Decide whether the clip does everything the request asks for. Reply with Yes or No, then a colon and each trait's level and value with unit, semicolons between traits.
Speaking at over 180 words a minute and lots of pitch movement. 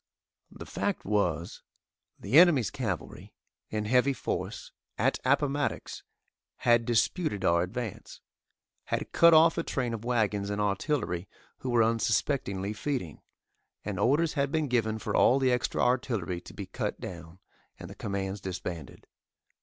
No: average, 140 wpm; wide, 5.7 semitones